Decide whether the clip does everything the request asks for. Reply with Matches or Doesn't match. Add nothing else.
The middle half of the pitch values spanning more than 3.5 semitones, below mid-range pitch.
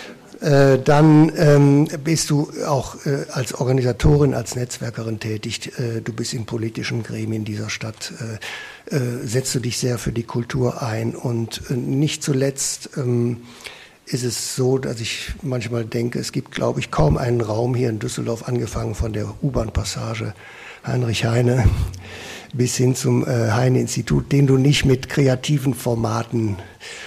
Doesn't match